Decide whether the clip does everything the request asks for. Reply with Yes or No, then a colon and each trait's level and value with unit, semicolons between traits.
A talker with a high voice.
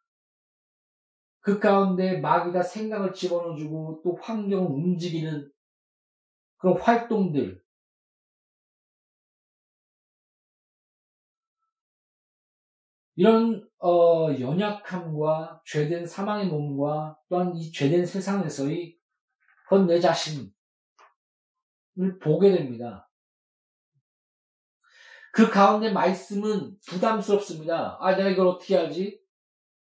No: medium, 180 Hz